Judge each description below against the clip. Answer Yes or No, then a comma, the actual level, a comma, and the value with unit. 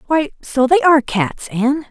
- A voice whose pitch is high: Yes, very high, 275 Hz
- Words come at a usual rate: Yes, average, 190 wpm